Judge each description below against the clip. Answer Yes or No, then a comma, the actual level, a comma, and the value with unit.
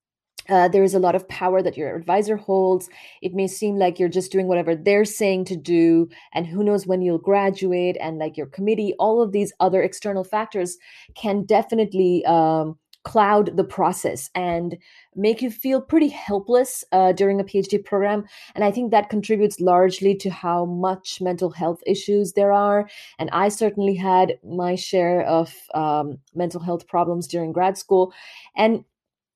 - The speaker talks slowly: No, average, 175 wpm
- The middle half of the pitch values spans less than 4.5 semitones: Yes, narrow, 2.6 semitones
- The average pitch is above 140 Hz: Yes, high, 190 Hz